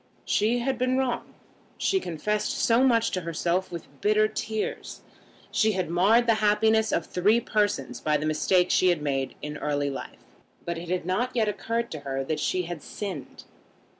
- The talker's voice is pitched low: No, high, 190 Hz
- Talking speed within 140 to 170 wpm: No, average, 180 wpm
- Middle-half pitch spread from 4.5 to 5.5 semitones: Yes, average, 5.1 semitones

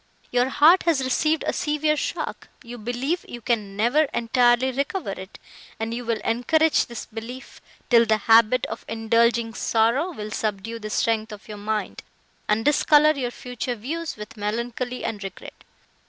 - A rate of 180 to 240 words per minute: No, average, 160 wpm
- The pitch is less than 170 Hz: No, high, 235 Hz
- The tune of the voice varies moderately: Yes, average, 3.2 semitones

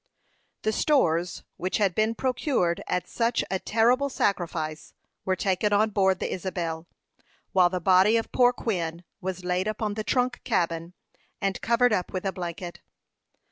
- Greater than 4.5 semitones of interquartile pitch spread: No, average, 4.0 semitones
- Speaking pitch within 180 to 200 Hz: Yes, high, 190 Hz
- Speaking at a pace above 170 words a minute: No, average, 155 wpm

